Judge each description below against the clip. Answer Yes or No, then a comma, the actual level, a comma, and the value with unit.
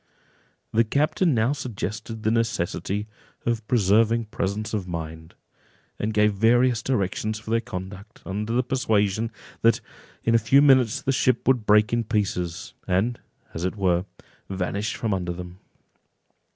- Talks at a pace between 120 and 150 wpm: Yes, average, 145 wpm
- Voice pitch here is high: No, low, 110 Hz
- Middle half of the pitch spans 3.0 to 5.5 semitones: Yes, average, 3.3 semitones